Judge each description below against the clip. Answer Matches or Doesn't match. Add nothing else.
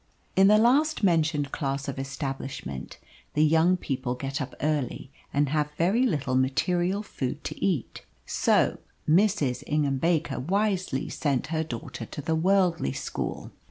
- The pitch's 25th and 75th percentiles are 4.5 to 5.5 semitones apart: Matches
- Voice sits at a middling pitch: Matches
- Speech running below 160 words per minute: Matches